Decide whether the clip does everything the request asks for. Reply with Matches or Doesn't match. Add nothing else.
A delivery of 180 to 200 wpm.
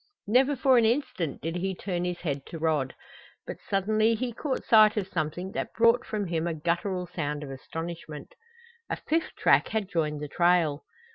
Matches